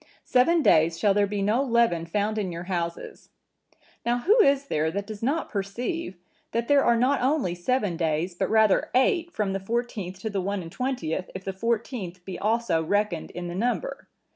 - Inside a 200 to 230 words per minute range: No, average, 190 wpm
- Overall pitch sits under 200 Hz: No, high, 205 Hz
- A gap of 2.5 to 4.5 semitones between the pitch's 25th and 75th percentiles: No, wide, 5.5 semitones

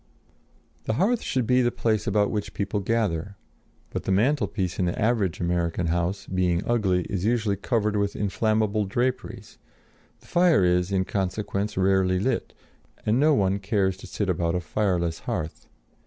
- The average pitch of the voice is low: Yes, low, 100 Hz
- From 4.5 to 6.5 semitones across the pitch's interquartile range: No, average, 3.2 semitones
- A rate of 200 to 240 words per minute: No, average, 165 wpm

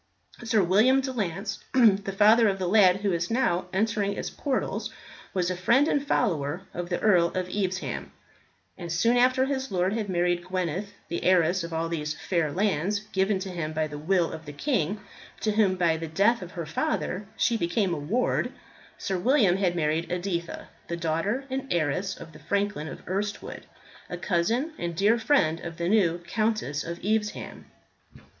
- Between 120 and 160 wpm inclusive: No, average, 180 wpm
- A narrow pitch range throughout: No, average, 4.1 semitones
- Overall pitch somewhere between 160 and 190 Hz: Yes, medium, 185 Hz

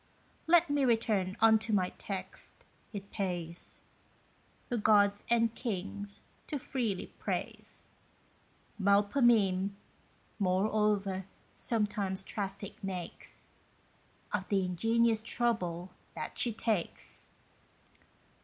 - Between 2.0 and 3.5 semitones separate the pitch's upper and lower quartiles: Yes, average, 3.1 semitones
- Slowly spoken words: Yes, slow, 90 wpm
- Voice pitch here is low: No, high, 205 Hz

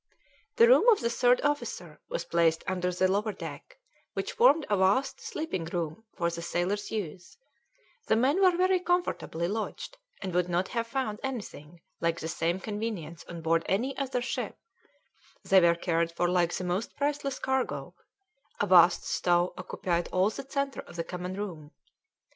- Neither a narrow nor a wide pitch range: No, wide, 7.3 semitones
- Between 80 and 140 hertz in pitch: No, high, 190 Hz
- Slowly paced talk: No, average, 170 wpm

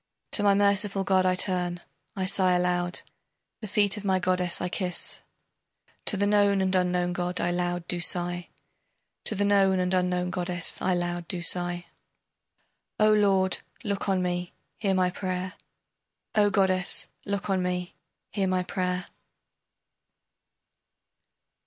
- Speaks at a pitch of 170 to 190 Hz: Yes, medium, 185 Hz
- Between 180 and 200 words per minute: No, average, 145 wpm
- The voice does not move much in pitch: Yes, narrow, 1.8 semitones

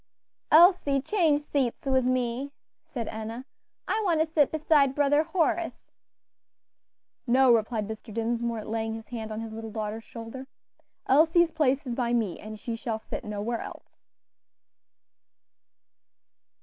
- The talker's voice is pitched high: Yes, high, 245 Hz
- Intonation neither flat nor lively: Yes, average, 4.6 semitones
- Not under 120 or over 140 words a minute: Yes, slow, 135 wpm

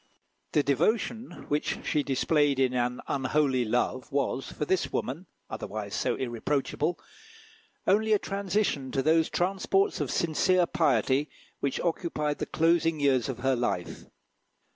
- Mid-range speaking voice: Yes, medium, 145 Hz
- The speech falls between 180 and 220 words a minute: No, slow, 135 wpm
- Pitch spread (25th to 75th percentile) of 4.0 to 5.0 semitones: Yes, average, 4.6 semitones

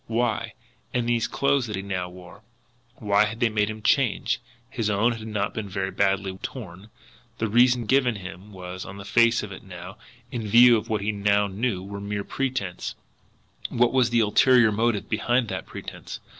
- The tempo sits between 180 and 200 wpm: Yes, average, 185 wpm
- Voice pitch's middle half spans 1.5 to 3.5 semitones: Yes, average, 3.2 semitones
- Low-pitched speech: Yes, low, 105 Hz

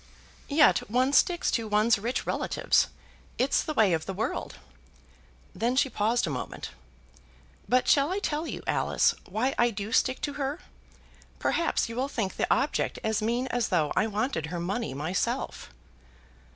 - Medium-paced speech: Yes, average, 160 wpm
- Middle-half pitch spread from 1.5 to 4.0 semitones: No, average, 4.5 semitones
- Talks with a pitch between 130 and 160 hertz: No, high, 235 Hz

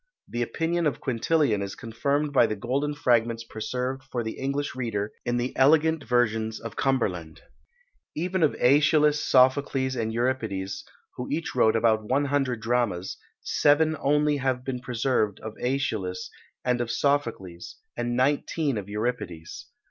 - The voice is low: Yes, low, 125 Hz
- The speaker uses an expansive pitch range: No, average, 4.1 semitones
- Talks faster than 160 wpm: No, average, 145 wpm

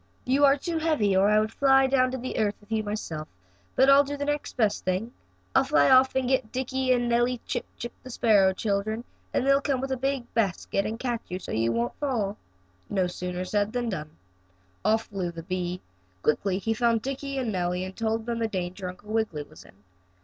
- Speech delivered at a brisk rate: Yes, fast, 215 wpm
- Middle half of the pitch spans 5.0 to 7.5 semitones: Yes, wide, 5.5 semitones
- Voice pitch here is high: Yes, high, 220 Hz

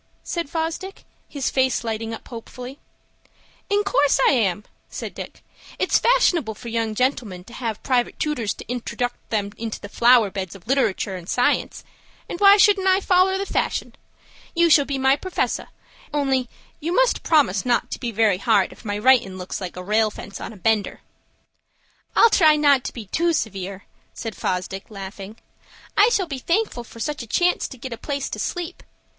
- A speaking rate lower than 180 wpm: No, average, 185 wpm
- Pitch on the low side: No, high, 245 Hz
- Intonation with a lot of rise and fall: Yes, wide, 6.7 semitones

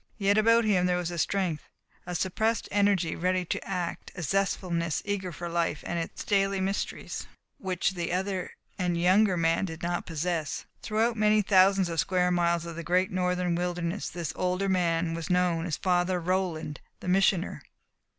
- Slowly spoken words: No, average, 170 wpm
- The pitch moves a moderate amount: No, narrow, 2.2 semitones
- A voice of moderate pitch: Yes, medium, 180 Hz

